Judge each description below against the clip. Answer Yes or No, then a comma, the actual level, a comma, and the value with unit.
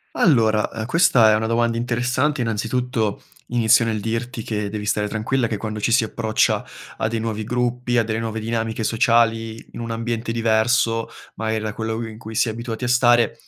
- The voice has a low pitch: Yes, low, 115 Hz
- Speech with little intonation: Yes, narrow, 1.4 semitones